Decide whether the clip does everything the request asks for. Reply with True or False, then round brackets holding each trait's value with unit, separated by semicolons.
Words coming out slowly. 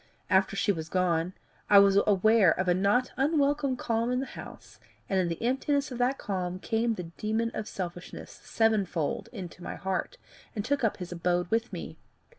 False (185 wpm)